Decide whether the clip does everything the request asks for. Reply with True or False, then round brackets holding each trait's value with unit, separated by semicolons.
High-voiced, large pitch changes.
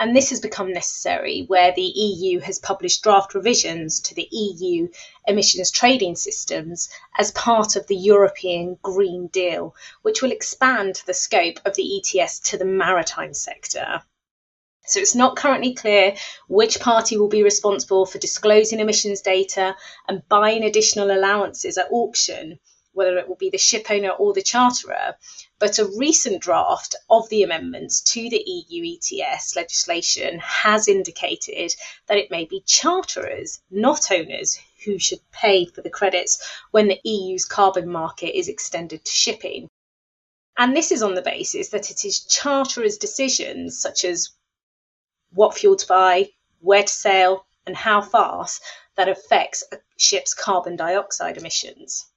True (205 Hz; 6.2 semitones)